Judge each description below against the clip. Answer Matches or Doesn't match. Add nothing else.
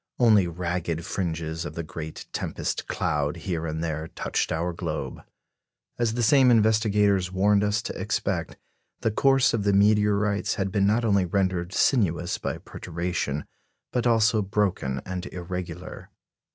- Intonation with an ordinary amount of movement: Matches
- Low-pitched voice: Matches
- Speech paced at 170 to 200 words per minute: Doesn't match